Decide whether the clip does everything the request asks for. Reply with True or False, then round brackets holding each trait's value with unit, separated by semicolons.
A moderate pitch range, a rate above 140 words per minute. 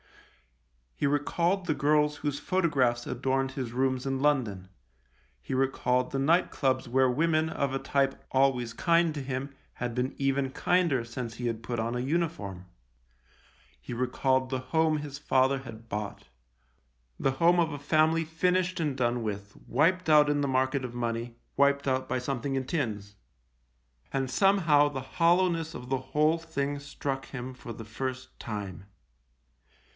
True (3.4 semitones; 165 wpm)